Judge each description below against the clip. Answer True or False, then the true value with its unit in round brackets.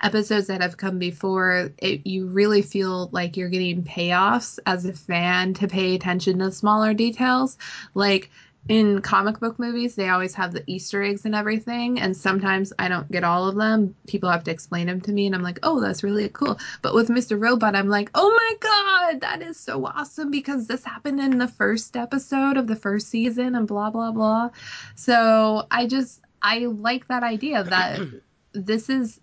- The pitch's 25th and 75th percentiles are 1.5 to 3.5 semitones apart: False (4.2 semitones)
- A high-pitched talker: True (210 Hz)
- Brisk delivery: False (195 wpm)